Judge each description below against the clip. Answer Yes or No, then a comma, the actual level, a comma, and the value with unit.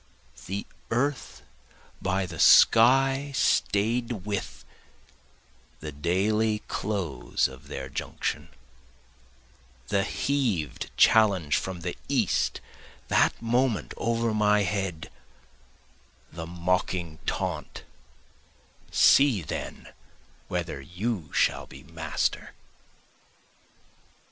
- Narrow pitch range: No, average, 5.3 semitones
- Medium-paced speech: No, slow, 85 wpm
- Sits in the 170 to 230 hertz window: No, very low, 95 Hz